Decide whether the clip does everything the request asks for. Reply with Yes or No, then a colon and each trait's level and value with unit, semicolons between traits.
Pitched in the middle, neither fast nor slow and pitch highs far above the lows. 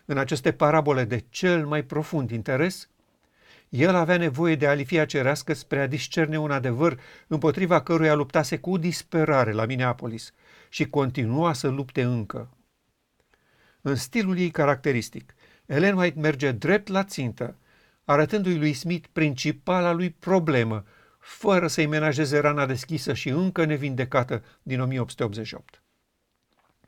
No: medium, 150 Hz; average, 125 wpm; average, 4.1 semitones